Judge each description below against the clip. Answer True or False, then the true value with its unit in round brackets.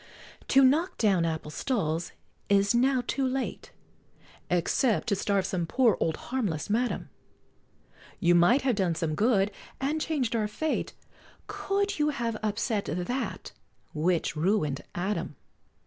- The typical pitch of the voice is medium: False (210 Hz)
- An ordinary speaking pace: False (130 wpm)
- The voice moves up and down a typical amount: False (6.9 semitones)